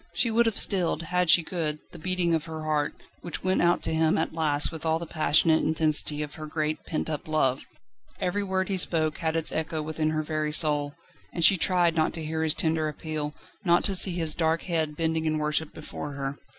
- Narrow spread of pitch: Yes, narrow, 1.7 semitones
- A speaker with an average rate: No, fast, 220 wpm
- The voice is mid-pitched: Yes, medium, 160 Hz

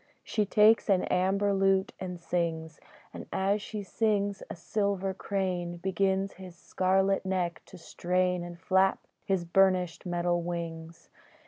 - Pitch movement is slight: Yes, narrow, 2.0 semitones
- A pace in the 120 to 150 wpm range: Yes, slow, 135 wpm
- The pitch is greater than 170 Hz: Yes, medium, 185 Hz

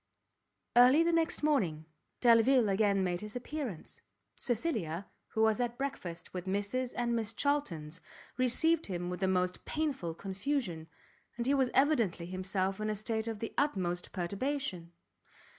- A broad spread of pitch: Yes, wide, 6.2 semitones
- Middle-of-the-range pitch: No, high, 215 Hz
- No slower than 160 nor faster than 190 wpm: No, average, 145 wpm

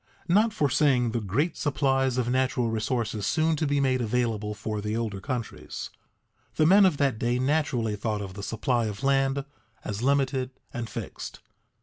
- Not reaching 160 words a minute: No, average, 175 wpm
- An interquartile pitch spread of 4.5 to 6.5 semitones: No, average, 4.0 semitones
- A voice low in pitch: Yes, low, 125 Hz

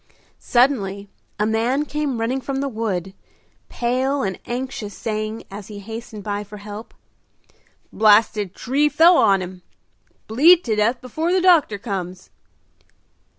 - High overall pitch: Yes, high, 225 Hz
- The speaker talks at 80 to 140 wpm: Yes, slow, 135 wpm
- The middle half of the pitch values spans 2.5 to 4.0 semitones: No, average, 4.6 semitones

